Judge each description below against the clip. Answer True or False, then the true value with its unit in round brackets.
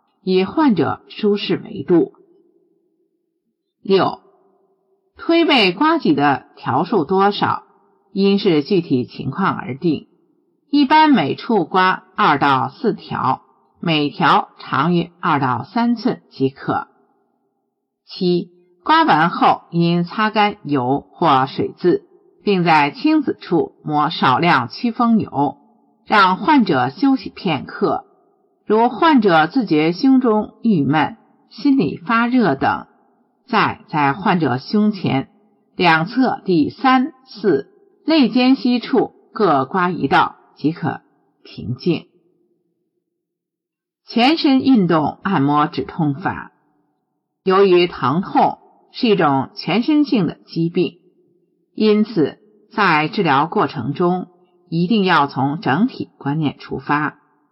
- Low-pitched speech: False (205 Hz)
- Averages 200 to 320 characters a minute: False (155 characters per minute)